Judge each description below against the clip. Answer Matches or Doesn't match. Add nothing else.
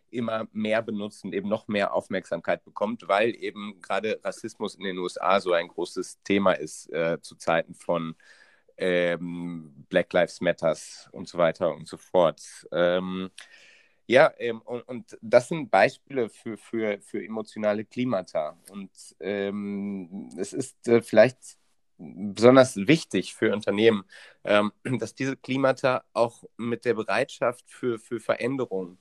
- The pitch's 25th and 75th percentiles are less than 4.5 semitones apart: Matches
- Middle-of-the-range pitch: Doesn't match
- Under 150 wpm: Matches